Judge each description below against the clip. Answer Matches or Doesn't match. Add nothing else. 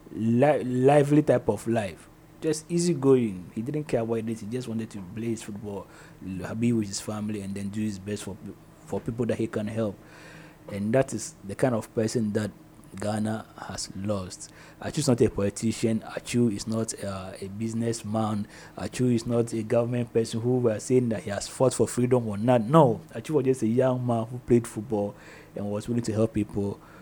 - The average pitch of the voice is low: Matches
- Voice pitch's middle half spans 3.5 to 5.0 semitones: Doesn't match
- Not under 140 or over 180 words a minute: Doesn't match